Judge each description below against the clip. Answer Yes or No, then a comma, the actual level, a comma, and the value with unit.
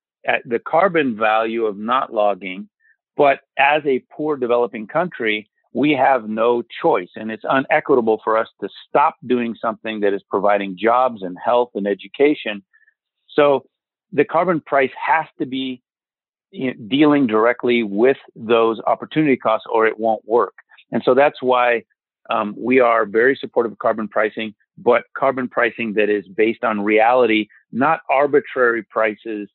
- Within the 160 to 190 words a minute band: No, average, 150 wpm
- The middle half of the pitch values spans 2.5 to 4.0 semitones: Yes, average, 3.4 semitones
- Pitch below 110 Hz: No, low, 115 Hz